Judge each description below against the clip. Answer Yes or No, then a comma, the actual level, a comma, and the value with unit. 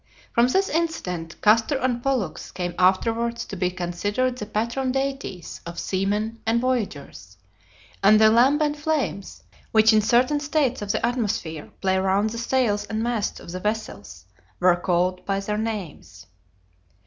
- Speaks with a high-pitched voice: Yes, high, 220 Hz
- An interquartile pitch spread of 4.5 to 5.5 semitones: Yes, average, 4.9 semitones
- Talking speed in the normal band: Yes, average, 150 wpm